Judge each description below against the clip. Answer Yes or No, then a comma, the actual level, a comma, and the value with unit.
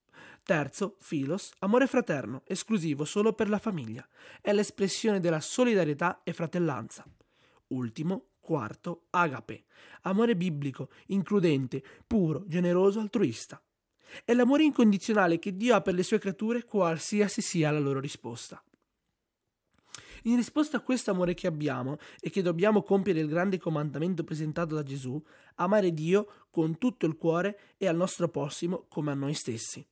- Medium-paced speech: Yes, average, 140 wpm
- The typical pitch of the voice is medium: Yes, medium, 180 Hz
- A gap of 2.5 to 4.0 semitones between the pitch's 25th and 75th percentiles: No, average, 5.1 semitones